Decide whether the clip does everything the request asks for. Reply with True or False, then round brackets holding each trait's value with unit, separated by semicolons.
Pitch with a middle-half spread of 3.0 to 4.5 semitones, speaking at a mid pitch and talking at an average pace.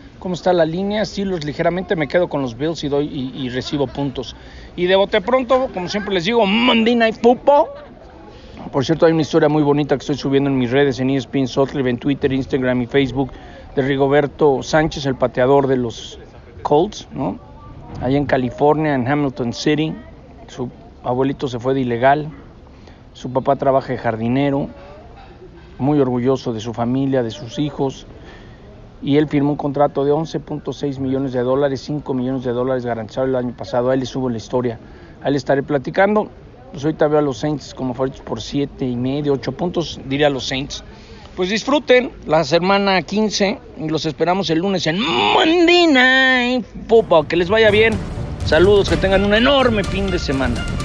False (5.4 semitones; 145 Hz; 180 wpm)